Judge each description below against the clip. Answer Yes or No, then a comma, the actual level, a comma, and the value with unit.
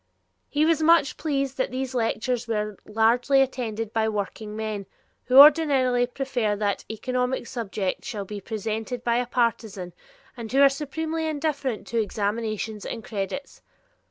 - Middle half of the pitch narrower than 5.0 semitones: Yes, average, 3.9 semitones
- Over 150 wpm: No, average, 145 wpm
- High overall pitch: Yes, high, 235 Hz